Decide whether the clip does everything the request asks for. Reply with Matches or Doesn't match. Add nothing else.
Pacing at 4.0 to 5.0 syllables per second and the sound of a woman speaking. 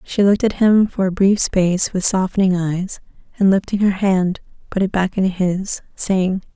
Matches